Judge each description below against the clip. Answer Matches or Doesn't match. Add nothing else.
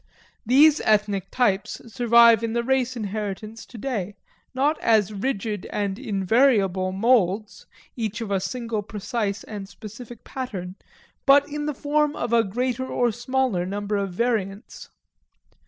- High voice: Matches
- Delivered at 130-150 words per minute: Matches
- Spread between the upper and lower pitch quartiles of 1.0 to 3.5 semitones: Doesn't match